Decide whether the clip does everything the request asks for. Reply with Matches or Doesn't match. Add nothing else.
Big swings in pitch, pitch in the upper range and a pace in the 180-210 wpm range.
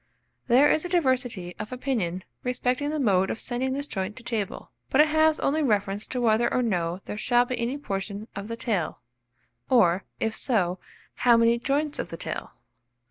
Doesn't match